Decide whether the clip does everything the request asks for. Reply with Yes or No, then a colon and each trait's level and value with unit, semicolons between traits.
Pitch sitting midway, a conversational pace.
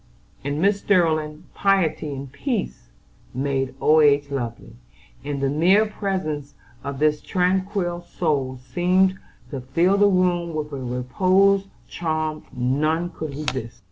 No: medium, 155 Hz; slow, 130 wpm